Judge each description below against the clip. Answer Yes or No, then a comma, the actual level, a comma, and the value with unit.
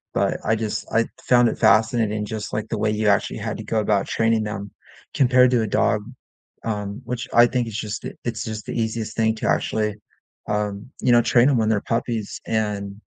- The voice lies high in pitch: No, low, 110 Hz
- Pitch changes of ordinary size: No, narrow, 1.8 semitones